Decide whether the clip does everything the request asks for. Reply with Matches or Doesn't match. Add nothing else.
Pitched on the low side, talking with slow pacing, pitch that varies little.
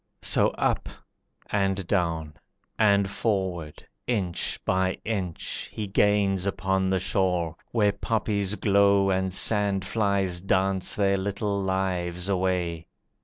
Matches